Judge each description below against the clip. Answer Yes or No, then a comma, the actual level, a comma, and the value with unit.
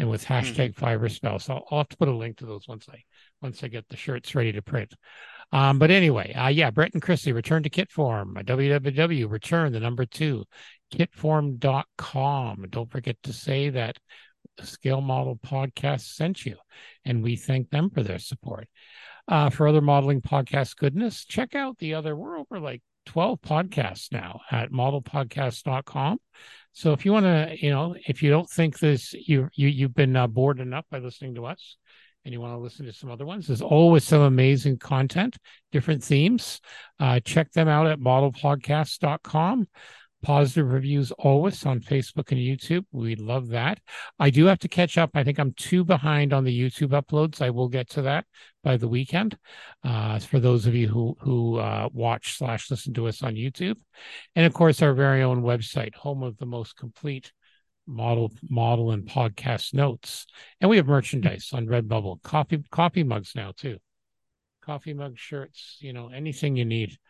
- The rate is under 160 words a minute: No, average, 185 wpm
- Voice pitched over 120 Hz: Yes, low, 135 Hz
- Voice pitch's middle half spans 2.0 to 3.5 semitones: No, average, 4.0 semitones